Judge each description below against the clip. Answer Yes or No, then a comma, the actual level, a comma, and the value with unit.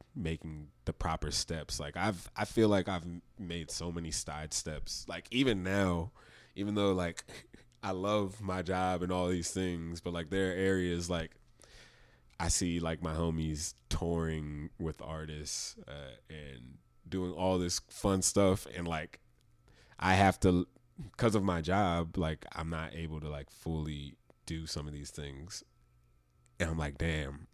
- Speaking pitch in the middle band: No, very low, 85 Hz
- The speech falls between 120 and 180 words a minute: Yes, average, 165 wpm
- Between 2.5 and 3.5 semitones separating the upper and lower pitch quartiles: Yes, average, 2.9 semitones